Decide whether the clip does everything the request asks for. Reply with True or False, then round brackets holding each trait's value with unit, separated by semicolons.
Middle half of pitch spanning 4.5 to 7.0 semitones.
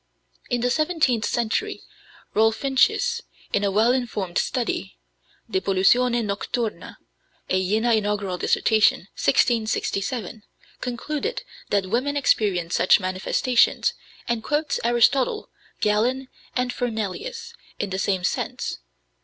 False (4.0 semitones)